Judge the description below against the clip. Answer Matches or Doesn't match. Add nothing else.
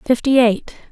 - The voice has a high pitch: Matches